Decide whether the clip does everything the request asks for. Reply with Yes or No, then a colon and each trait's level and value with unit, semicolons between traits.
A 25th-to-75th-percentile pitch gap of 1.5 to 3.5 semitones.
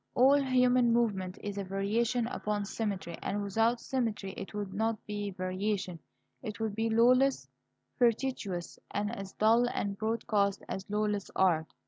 Yes: average, 2.9 semitones